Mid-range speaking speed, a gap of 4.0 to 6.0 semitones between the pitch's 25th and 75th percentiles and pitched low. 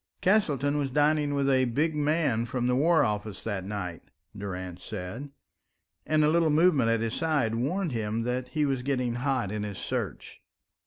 Yes: average, 175 wpm; average, 5.2 semitones; low, 130 Hz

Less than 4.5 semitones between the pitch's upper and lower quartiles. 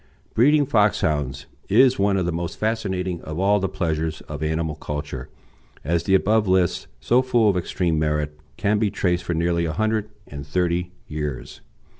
No: average, 4.8 semitones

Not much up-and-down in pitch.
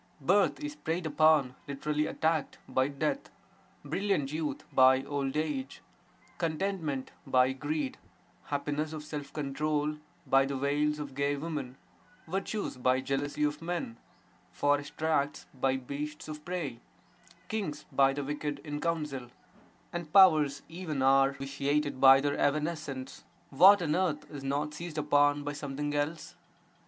Yes: narrow, 2.3 semitones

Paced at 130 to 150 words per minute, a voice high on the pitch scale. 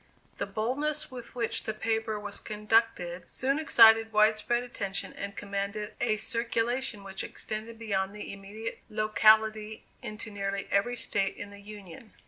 Yes: average, 145 wpm; high, 215 Hz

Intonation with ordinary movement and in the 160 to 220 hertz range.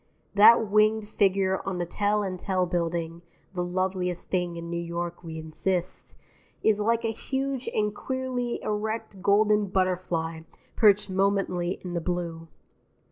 Yes: average, 3.3 semitones; high, 190 Hz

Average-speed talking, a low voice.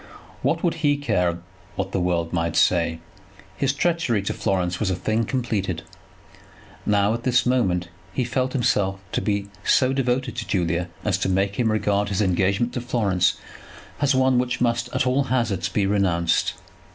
Yes: average, 170 wpm; low, 105 Hz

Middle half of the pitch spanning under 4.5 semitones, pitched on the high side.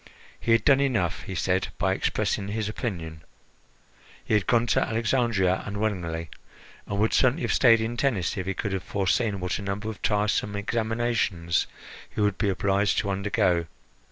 No: average, 2.9 semitones; low, 105 Hz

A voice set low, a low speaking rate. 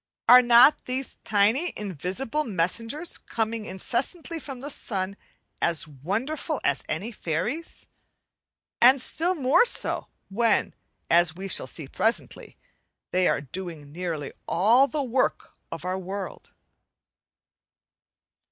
No: high, 220 Hz; slow, 115 wpm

